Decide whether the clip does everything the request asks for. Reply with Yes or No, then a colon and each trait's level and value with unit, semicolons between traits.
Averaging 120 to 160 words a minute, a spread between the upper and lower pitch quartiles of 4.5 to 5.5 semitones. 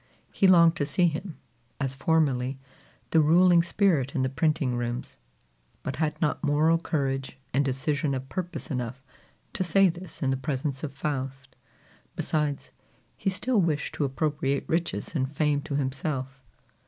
No: average, 155 wpm; average, 3.5 semitones